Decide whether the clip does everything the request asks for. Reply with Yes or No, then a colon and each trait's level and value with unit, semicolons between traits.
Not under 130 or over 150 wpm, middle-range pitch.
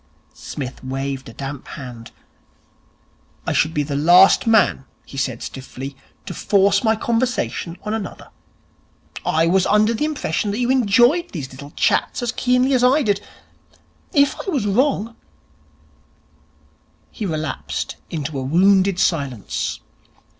Yes: average, 140 wpm; medium, 180 Hz